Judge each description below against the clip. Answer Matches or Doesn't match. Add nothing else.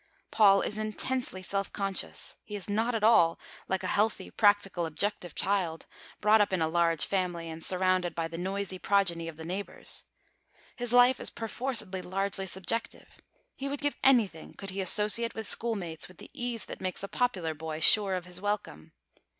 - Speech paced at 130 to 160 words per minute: Doesn't match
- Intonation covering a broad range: Doesn't match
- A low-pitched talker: Doesn't match